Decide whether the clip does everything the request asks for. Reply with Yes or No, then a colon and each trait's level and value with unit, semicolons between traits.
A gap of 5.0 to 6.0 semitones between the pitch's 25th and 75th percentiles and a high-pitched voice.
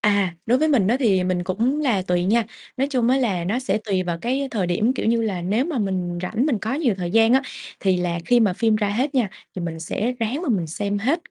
Yes: average, 5.3 semitones; high, 215 Hz